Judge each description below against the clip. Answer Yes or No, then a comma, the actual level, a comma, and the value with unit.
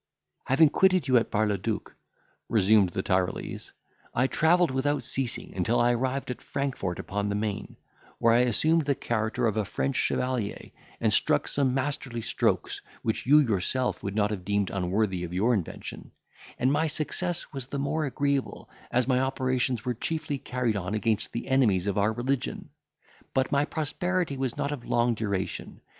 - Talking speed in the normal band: Yes, average, 175 wpm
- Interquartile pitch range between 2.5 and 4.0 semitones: No, average, 4.7 semitones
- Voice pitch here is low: Yes, low, 125 Hz